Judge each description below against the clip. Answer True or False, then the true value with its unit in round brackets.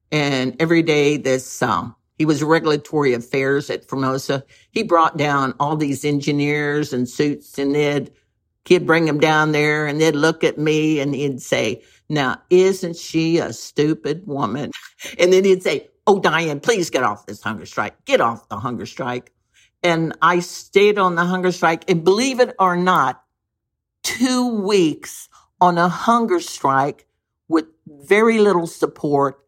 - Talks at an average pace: True (160 wpm)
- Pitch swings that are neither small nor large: True (4.3 semitones)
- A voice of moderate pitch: True (155 Hz)